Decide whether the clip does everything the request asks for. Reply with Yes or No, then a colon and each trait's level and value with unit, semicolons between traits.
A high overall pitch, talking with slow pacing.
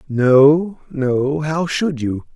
No: medium, 145 Hz; slow, 125 wpm